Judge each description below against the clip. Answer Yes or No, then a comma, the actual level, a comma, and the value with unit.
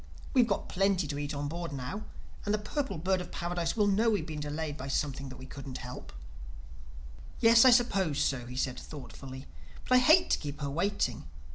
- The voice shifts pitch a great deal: Yes, wide, 6.8 semitones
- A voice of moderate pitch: Yes, medium, 160 Hz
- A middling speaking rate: No, fast, 215 wpm